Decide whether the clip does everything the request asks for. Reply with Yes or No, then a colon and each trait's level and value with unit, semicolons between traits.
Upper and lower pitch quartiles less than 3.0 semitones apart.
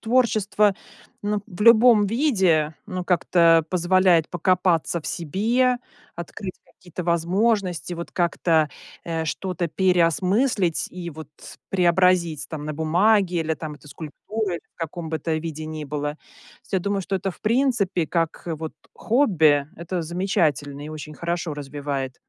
No: average, 3.6 semitones